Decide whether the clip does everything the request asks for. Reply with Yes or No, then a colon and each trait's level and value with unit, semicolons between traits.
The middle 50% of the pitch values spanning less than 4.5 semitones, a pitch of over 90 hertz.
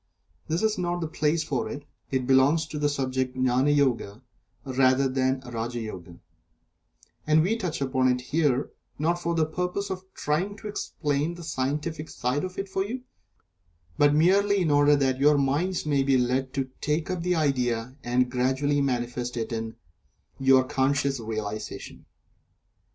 Yes: average, 4.1 semitones; medium, 140 Hz